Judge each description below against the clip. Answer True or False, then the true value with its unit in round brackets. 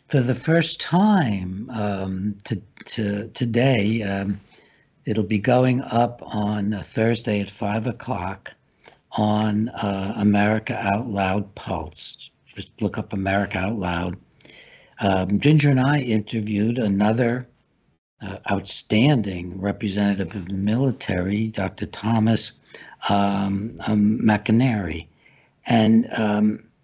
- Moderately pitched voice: False (105 Hz)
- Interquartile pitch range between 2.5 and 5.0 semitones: True (2.8 semitones)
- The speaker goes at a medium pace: False (110 wpm)